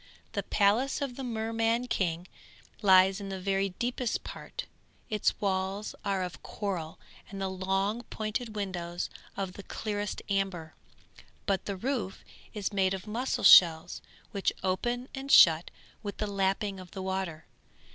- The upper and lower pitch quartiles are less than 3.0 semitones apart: Yes, narrow, 2.4 semitones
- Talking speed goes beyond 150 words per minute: No, average, 145 wpm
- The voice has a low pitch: No, high, 195 Hz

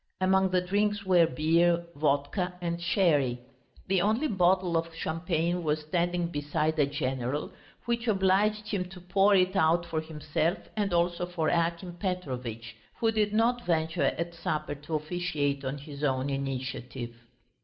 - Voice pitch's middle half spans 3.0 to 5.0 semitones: Yes, average, 3.8 semitones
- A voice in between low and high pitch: Yes, medium, 170 Hz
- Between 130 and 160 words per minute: Yes, average, 150 wpm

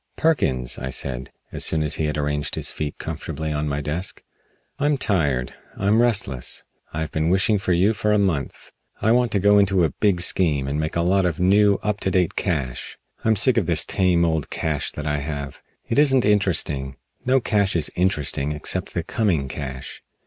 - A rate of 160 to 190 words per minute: No, average, 200 wpm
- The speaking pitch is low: Yes, very low, 85 Hz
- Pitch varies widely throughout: Yes, wide, 5.7 semitones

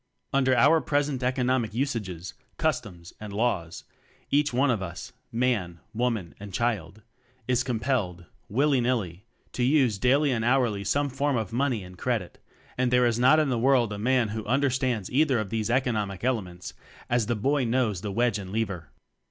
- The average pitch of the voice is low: Yes, low, 120 Hz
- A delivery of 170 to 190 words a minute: Yes, average, 175 wpm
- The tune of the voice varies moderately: Yes, average, 4.1 semitones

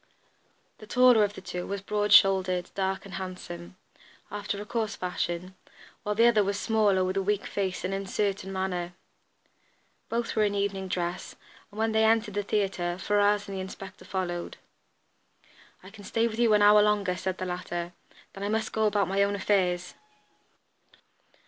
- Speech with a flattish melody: Yes, narrow, 2.0 semitones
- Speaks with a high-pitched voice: Yes, high, 200 Hz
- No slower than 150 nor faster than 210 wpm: Yes, average, 175 wpm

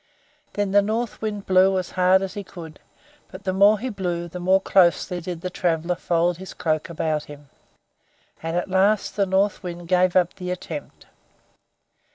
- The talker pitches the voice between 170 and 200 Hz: Yes, medium, 185 Hz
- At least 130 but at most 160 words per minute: No, average, 180 wpm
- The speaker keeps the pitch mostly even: Yes, narrow, 2.1 semitones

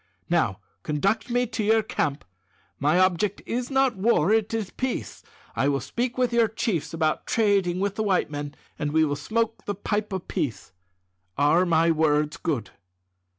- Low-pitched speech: No, high, 190 Hz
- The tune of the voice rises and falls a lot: Yes, wide, 6.4 semitones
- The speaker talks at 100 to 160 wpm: No, average, 170 wpm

